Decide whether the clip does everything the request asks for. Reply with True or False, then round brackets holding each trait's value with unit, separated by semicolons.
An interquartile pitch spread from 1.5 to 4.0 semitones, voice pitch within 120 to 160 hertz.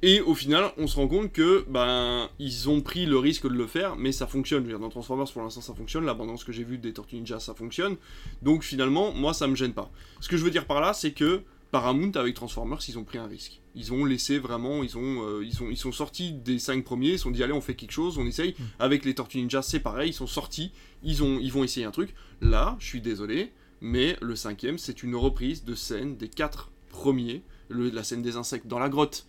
True (3.5 semitones; 130 Hz)